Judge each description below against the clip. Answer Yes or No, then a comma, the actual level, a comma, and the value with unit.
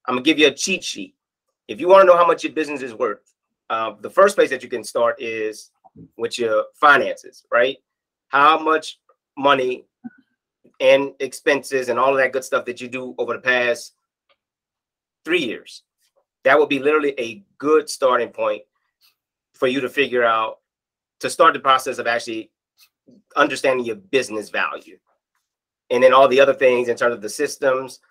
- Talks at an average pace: Yes, average, 175 wpm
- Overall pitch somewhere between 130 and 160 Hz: Yes, medium, 140 Hz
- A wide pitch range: Yes, wide, 7.4 semitones